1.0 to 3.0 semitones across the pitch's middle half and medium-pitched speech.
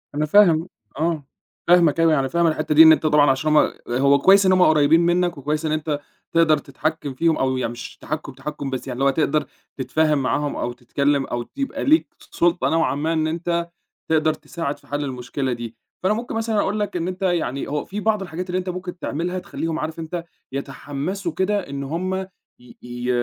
No: average, 3.9 semitones; medium, 155 Hz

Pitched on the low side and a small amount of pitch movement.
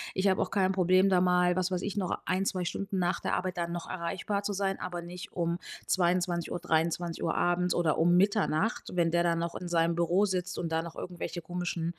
No: medium, 180 Hz; narrow, 1.5 semitones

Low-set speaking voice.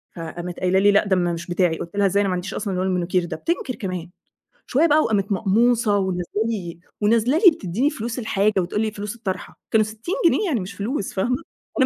No: high, 200 Hz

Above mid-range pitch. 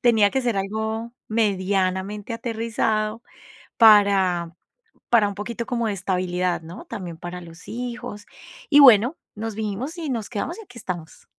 Yes: high, 215 Hz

